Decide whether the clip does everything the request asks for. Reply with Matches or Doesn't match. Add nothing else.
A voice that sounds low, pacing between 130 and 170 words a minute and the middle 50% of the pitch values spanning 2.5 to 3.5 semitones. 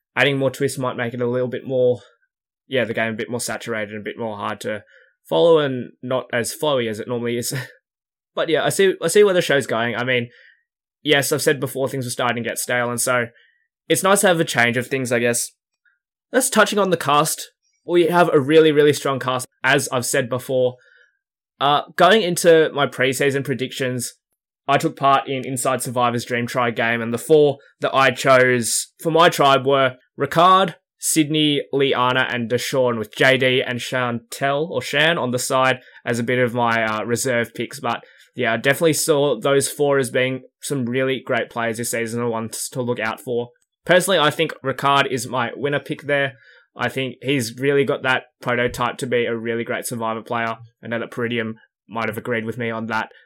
Doesn't match